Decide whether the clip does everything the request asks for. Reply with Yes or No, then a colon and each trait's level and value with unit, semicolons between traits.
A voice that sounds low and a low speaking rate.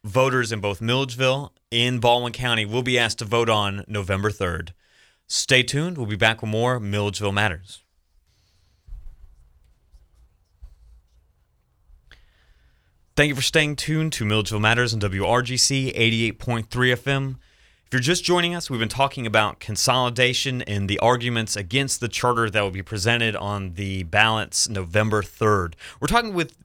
No: low, 110 Hz; average, 145 wpm